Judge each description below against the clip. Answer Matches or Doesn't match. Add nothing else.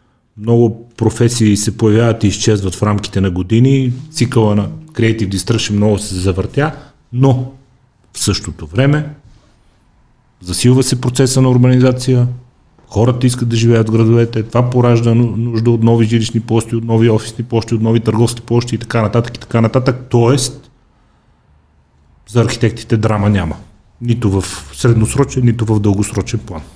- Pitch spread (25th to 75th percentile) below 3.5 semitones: Matches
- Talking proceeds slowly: Doesn't match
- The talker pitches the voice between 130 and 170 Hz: Doesn't match